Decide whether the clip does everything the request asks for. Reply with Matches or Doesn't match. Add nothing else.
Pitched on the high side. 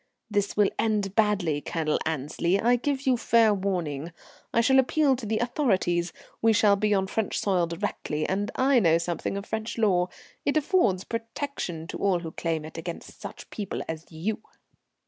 Matches